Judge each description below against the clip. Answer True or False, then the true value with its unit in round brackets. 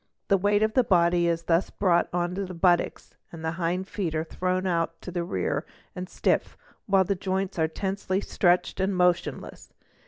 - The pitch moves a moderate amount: False (2.0 semitones)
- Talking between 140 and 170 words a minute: False (185 wpm)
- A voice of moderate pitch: True (180 Hz)